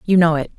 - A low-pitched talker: No, medium, 165 Hz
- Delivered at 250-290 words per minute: No, fast, 310 wpm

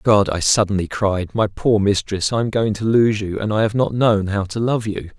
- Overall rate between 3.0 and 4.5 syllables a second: No, 4.9 syllables/s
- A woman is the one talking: No, male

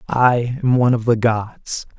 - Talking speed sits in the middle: Yes, average, 180 wpm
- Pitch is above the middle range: No, low, 120 Hz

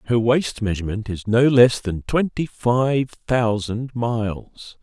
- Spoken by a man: Yes, male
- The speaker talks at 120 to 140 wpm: Yes, slow, 135 wpm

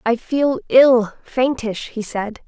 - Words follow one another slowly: Yes, slow, 120 wpm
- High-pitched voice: Yes, high, 240 Hz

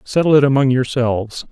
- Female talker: No, male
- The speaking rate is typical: Yes, average, 160 wpm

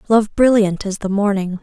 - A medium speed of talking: Yes, average, 185 wpm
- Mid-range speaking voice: No, high, 205 Hz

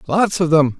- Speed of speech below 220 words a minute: No, fast, 225 wpm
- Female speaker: No, male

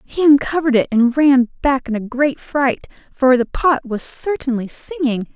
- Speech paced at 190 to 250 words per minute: No, average, 180 wpm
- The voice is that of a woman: Yes, female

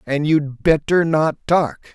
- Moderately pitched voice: Yes, medium, 150 Hz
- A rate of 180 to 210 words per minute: No, average, 155 wpm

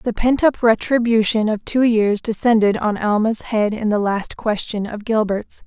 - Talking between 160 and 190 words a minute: Yes, average, 180 wpm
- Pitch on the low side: No, high, 220 Hz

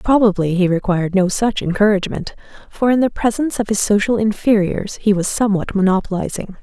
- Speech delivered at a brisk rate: No, average, 165 wpm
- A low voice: No, high, 205 Hz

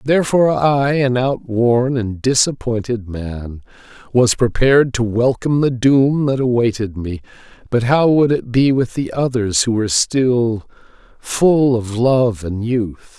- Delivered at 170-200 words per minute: No, average, 145 wpm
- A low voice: Yes, low, 120 Hz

